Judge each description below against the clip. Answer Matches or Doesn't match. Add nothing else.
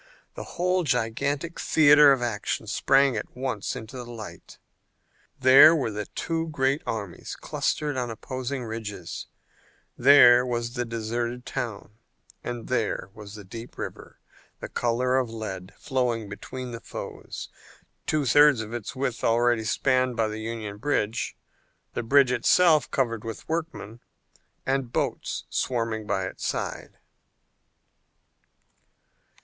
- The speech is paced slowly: Matches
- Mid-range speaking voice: Doesn't match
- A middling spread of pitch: Matches